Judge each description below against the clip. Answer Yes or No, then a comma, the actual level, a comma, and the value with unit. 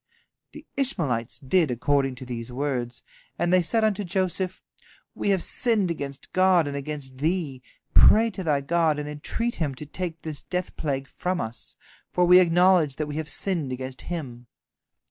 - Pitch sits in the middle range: Yes, medium, 155 Hz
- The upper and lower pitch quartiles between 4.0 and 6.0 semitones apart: Yes, average, 5.1 semitones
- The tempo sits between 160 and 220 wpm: Yes, average, 170 wpm